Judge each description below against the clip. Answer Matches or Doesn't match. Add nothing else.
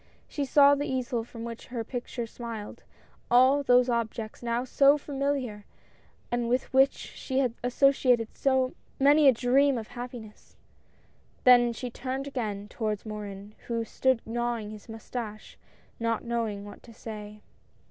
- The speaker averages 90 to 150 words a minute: Matches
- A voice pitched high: Matches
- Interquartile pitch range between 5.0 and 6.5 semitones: Doesn't match